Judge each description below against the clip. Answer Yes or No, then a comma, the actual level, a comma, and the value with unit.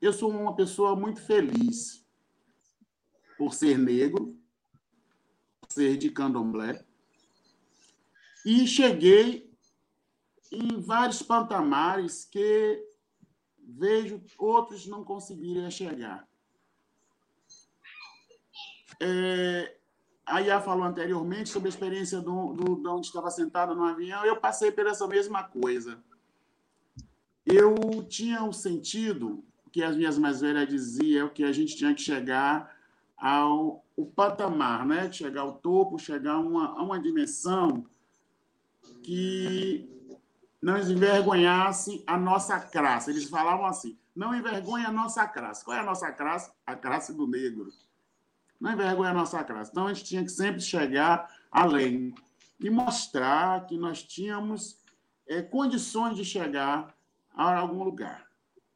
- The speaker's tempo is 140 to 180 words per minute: No, average, 125 wpm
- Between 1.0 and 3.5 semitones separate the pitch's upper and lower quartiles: No, wide, 5.4 semitones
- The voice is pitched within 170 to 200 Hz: Yes, high, 190 Hz